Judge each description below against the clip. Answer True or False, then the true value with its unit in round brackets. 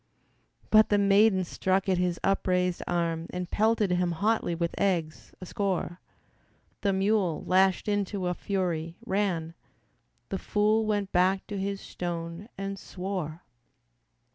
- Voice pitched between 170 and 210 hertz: True (190 Hz)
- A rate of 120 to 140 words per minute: True (135 wpm)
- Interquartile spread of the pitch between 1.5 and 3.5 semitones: True (2.4 semitones)